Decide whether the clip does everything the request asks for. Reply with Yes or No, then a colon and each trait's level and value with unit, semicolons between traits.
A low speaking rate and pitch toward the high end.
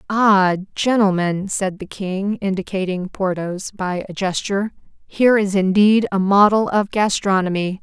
Yes: slow, 130 wpm; high, 195 Hz